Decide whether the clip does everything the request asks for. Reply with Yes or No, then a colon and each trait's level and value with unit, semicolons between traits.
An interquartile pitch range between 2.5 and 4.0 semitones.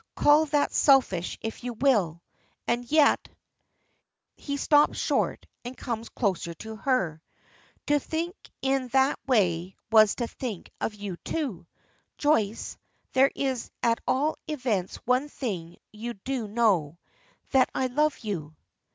No: average, 5.3 semitones